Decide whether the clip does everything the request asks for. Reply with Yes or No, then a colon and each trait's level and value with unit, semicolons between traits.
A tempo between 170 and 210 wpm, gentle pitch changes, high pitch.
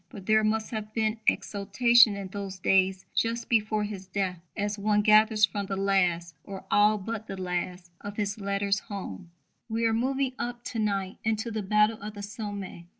Yes: average, 185 wpm; narrow, 1.9 semitones; high, 205 Hz